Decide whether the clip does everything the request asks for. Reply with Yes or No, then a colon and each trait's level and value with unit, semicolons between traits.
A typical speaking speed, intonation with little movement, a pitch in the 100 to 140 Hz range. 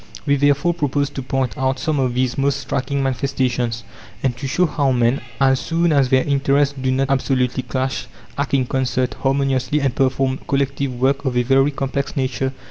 Yes: average, 185 wpm; narrow, 1.3 semitones; low, 135 Hz